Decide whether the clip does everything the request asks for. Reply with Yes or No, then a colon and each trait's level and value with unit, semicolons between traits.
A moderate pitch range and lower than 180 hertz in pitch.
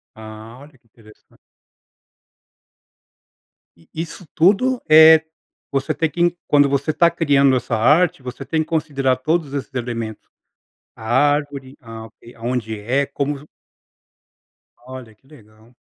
Yes: average, 4.8 semitones; low, 135 Hz